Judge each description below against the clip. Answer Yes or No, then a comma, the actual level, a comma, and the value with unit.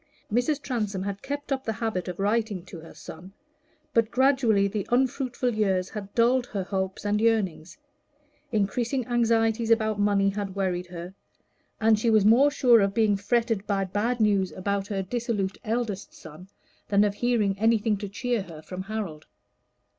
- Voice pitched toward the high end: Yes, high, 210 Hz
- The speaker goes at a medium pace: Yes, average, 165 wpm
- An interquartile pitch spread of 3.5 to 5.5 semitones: No, average, 3.1 semitones